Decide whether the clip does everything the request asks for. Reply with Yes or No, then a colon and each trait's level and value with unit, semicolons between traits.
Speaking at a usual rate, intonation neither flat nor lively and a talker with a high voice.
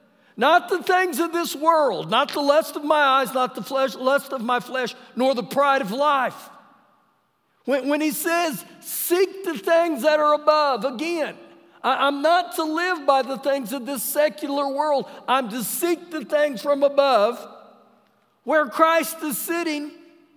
Yes: average, 170 wpm; average, 3.2 semitones; very high, 295 Hz